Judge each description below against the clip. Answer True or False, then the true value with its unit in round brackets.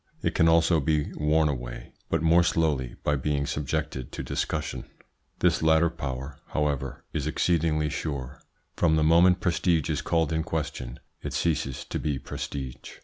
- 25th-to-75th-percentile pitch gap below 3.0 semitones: True (2.6 semitones)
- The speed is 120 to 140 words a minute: False (155 wpm)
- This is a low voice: True (75 Hz)